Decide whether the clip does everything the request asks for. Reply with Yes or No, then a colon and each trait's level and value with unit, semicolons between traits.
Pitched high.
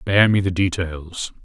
No: very low, 90 Hz